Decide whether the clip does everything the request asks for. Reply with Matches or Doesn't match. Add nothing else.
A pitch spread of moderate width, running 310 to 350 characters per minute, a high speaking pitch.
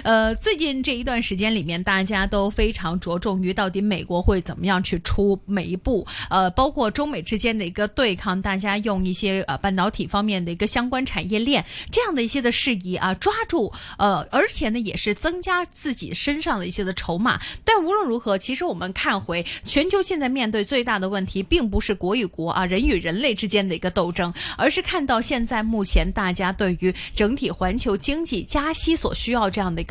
Doesn't match